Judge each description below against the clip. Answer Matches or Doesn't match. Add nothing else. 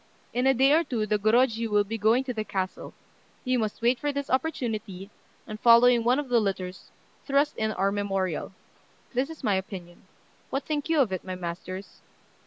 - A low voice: Doesn't match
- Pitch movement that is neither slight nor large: Matches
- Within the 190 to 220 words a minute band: Matches